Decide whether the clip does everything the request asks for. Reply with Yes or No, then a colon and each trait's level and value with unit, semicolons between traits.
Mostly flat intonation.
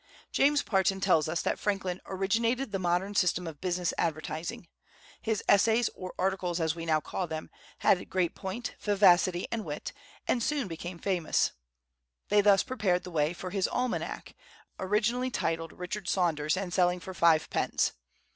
No: average, 3.2 semitones